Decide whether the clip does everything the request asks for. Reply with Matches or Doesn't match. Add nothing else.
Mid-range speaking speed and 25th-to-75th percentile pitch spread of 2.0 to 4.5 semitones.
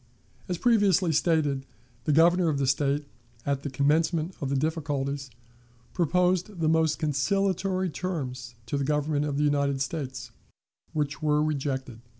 Matches